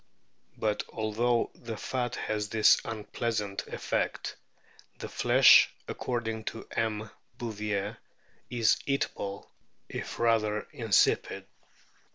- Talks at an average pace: No, slow, 100 wpm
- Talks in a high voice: No, low, 110 Hz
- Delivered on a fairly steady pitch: Yes, narrow, 1.8 semitones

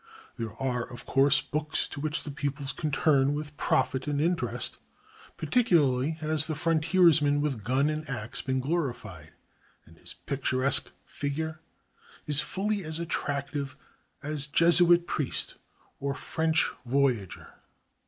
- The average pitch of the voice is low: No, medium, 145 Hz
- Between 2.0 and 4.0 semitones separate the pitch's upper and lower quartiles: Yes, average, 2.9 semitones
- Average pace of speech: No, slow, 130 wpm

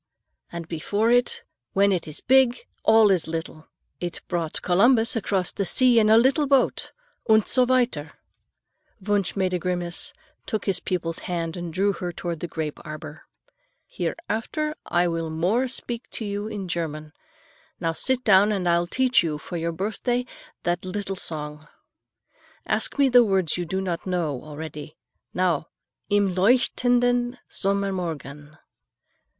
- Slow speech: No, average, 150 wpm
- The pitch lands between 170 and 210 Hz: Yes, medium, 185 Hz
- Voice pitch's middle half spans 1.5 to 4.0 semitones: No, average, 5.2 semitones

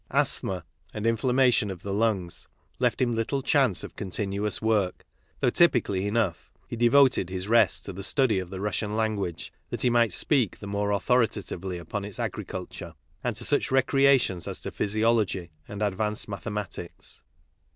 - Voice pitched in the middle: No, low, 105 Hz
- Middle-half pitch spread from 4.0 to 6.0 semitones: No, average, 3.5 semitones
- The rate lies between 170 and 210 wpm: No, average, 160 wpm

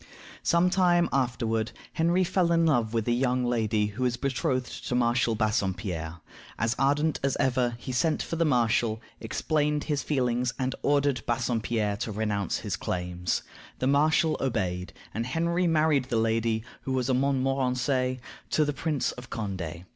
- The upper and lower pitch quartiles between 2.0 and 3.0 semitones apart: No, average, 4.4 semitones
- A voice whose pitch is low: Yes, low, 125 Hz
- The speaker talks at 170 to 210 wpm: No, average, 160 wpm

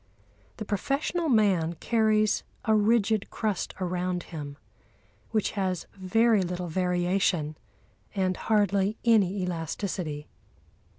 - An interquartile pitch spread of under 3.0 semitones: No, average, 3.3 semitones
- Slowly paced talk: Yes, slow, 100 wpm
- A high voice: Yes, high, 195 Hz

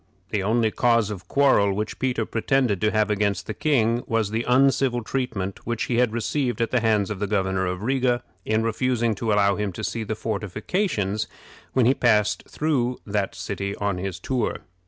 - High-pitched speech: No, low, 110 Hz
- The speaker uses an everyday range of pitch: Yes, average, 3.2 semitones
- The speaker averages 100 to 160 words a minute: No, average, 190 wpm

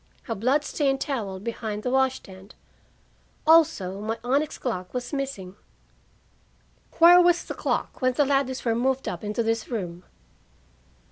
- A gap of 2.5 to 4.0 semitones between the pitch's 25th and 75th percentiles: No, average, 4.8 semitones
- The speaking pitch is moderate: No, high, 245 Hz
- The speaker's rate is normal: Yes, average, 145 wpm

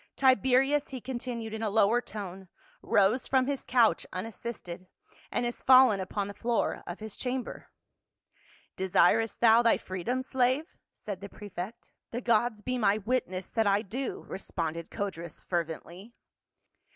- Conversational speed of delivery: Yes, average, 150 wpm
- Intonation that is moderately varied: Yes, average, 4.4 semitones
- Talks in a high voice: Yes, high, 220 Hz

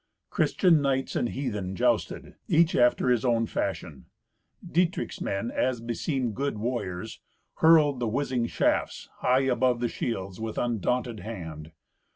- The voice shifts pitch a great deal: No, average, 3.3 semitones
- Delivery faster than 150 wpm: No, slow, 135 wpm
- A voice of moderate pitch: No, low, 120 Hz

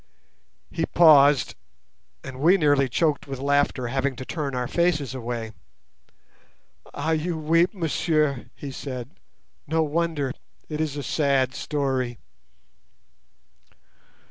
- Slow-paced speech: Yes, slow, 110 wpm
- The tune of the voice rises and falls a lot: No, average, 3.1 semitones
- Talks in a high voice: No, medium, 145 Hz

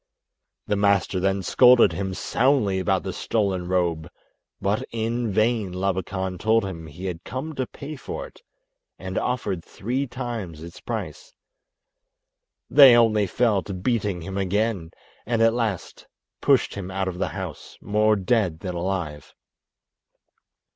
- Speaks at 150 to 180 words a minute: No, average, 140 wpm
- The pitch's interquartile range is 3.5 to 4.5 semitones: Yes, average, 4.0 semitones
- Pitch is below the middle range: Yes, low, 100 Hz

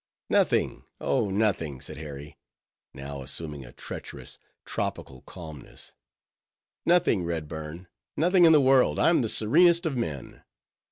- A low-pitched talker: Yes, very low, 85 Hz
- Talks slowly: Yes, slow, 115 wpm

